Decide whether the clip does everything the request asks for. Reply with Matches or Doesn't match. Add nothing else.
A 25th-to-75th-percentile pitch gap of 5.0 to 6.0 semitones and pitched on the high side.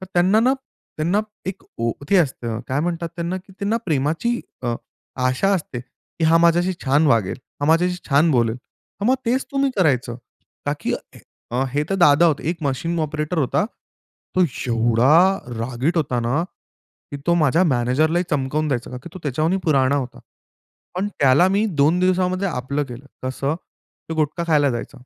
Doesn't match